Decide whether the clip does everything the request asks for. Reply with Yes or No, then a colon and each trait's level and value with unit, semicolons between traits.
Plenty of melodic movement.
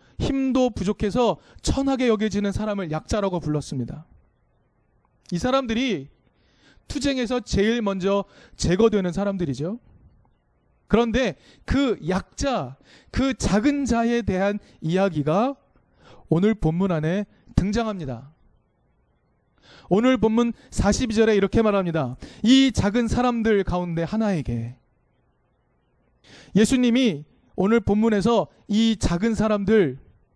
No: average, 4.9 semitones